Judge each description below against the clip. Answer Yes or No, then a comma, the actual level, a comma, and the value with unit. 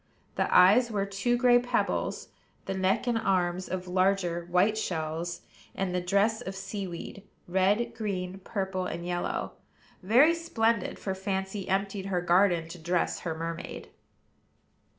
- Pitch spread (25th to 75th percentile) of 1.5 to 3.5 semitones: Yes, narrow, 2.6 semitones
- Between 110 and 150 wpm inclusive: Yes, average, 145 wpm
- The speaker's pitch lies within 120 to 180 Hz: No, high, 190 Hz